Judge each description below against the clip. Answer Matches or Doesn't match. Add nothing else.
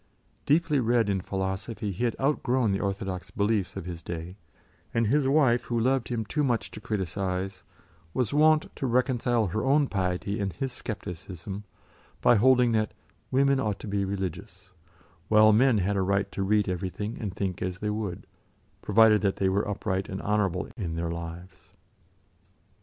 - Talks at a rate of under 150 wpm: Doesn't match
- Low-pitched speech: Matches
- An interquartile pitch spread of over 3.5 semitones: Matches